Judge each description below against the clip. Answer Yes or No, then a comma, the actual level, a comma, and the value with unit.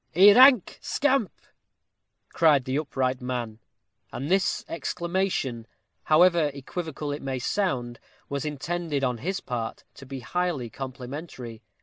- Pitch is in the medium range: Yes, medium, 145 Hz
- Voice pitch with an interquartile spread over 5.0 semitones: Yes, wide, 5.5 semitones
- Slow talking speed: Yes, slow, 120 wpm